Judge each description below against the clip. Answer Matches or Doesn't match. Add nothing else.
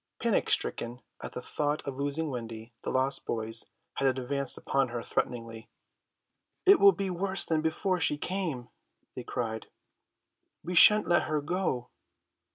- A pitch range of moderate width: Doesn't match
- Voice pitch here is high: Doesn't match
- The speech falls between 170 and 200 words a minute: Doesn't match